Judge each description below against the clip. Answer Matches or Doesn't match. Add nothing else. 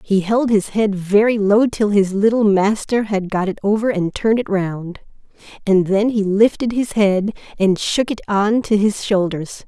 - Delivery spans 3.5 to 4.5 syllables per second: Matches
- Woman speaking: Matches